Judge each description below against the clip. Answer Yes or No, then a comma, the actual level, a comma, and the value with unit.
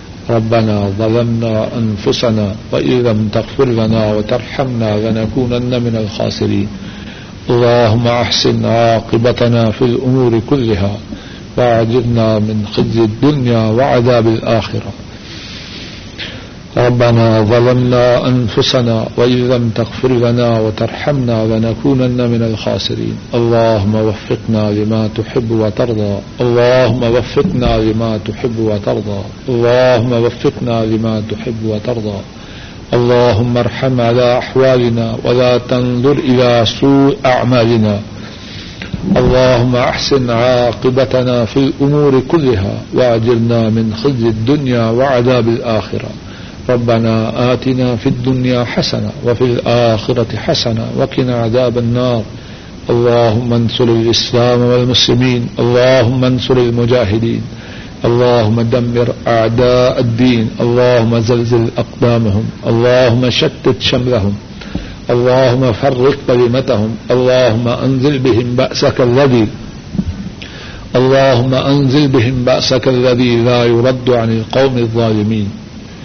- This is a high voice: No, low, 120 Hz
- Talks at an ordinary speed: No, slow, 95 wpm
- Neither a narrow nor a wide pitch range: No, narrow, 2.1 semitones